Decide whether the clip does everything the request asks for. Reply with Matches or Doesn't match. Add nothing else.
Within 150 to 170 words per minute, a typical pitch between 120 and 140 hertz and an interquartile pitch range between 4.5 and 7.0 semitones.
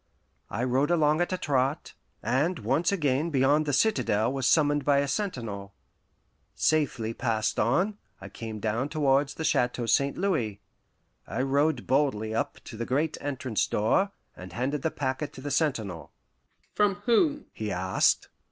Matches